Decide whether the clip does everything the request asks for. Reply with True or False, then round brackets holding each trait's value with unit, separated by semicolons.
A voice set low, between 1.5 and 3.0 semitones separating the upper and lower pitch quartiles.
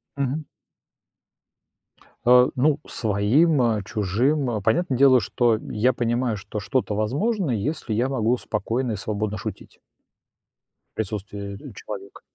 False (115 Hz; 3.8 semitones)